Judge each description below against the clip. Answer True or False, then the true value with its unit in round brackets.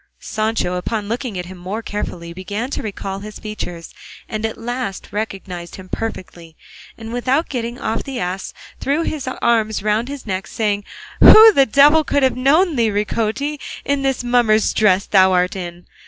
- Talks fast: False (175 wpm)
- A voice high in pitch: True (220 Hz)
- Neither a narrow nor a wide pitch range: True (4.8 semitones)